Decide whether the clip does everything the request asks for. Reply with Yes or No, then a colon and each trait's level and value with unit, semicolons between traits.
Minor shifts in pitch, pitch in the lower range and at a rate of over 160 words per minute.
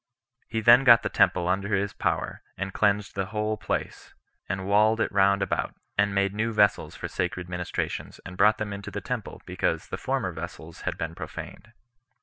Yes: narrow, 2.3 semitones; low, 100 Hz; average, 185 wpm